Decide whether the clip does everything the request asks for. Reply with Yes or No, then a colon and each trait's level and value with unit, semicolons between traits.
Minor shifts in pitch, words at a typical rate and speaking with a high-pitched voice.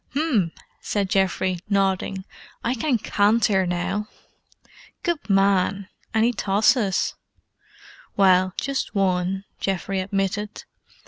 No: narrow, 2.2 semitones; slow, 90 wpm; high, 195 Hz